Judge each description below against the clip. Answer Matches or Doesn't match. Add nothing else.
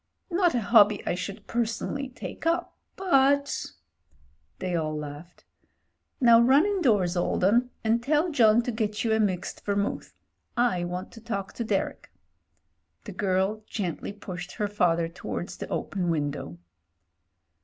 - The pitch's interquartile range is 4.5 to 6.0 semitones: Matches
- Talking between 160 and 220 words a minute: Doesn't match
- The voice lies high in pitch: Matches